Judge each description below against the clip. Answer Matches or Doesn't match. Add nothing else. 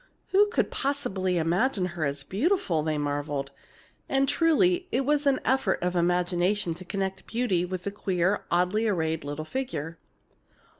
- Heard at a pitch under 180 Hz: Doesn't match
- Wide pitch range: Matches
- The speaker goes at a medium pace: Matches